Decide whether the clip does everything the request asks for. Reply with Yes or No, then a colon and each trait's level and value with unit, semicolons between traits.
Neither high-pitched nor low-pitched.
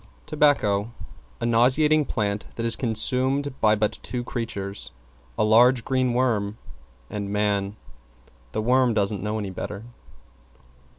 No: low, 115 Hz